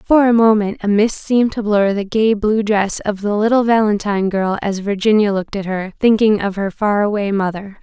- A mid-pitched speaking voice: No, high, 210 Hz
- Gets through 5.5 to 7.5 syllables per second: No, 5.2 syllables/s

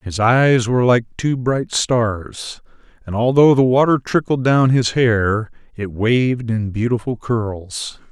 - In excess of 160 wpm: No, average, 150 wpm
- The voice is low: Yes, low, 120 Hz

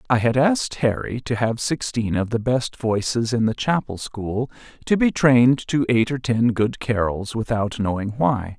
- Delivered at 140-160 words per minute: No, average, 190 wpm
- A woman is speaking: No, male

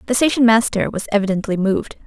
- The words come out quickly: No, average, 175 wpm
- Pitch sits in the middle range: No, high, 215 Hz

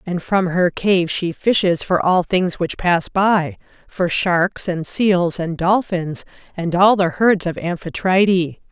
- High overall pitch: No, medium, 180 Hz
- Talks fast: No, average, 165 wpm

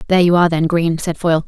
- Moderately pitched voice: Yes, medium, 170 Hz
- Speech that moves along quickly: Yes, fast, 285 wpm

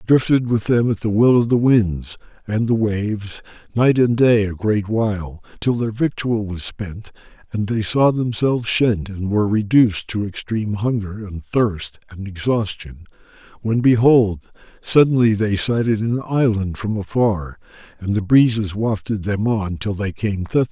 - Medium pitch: No, low, 110 Hz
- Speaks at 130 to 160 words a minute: No, average, 170 wpm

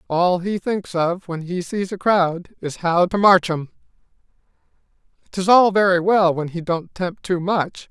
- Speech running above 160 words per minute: Yes, average, 180 wpm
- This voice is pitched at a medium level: Yes, medium, 180 Hz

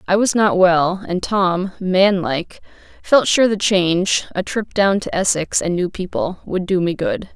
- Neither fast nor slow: Yes, average, 190 wpm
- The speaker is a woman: Yes, female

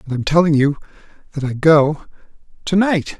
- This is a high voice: No, medium, 155 Hz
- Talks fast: No, average, 150 wpm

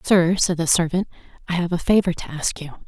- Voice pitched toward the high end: No, medium, 170 Hz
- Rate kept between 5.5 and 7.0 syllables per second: Yes, 5.6 syllables/s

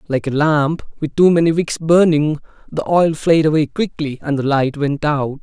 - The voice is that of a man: Yes, male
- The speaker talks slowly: No, average, 200 wpm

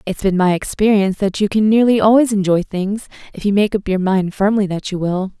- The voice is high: Yes, high, 200 Hz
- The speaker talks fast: Yes, fast, 235 wpm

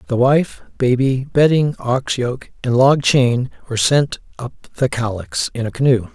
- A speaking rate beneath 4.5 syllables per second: Yes, 4.3 syllables/s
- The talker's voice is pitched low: Yes, low, 125 Hz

